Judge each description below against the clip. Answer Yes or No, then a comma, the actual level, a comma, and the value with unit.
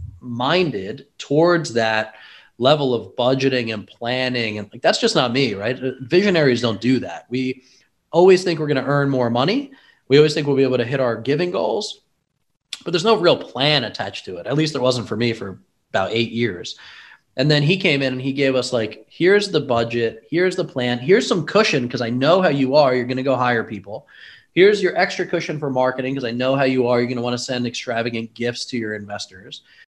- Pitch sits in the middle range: No, low, 130 Hz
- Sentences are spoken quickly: Yes, fast, 225 wpm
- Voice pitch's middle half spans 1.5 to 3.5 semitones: No, average, 4.6 semitones